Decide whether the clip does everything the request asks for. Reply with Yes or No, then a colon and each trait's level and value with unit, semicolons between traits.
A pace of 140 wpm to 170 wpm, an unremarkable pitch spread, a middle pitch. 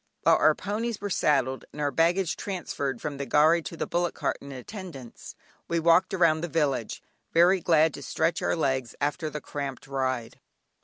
No: average, 185 wpm; average, 3.9 semitones; medium, 155 Hz